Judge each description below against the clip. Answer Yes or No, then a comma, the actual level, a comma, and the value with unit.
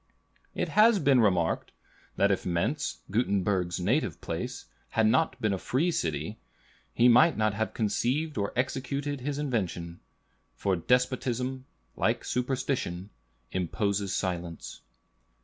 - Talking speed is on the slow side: Yes, slow, 120 wpm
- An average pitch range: No, wide, 5.9 semitones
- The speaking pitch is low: Yes, low, 115 Hz